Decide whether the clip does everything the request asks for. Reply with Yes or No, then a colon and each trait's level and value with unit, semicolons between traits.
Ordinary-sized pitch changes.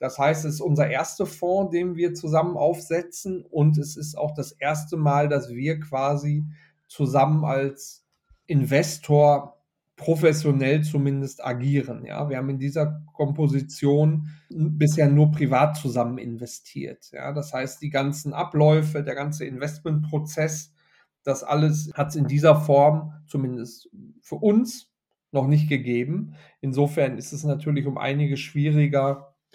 No: narrow, 1.8 semitones